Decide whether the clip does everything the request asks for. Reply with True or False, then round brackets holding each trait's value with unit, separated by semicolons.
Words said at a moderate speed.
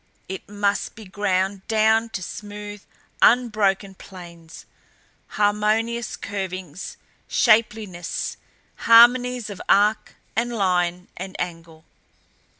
False (90 wpm)